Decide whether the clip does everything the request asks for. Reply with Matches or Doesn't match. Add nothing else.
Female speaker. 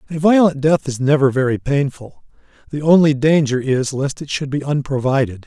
Doesn't match